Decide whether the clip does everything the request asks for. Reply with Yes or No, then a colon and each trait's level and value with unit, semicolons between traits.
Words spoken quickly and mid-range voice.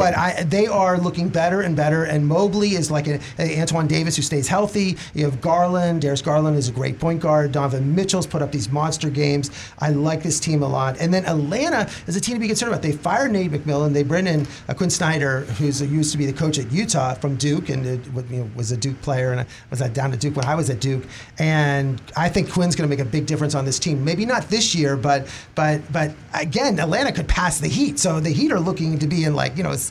Yes: fast, 255 wpm; medium, 150 Hz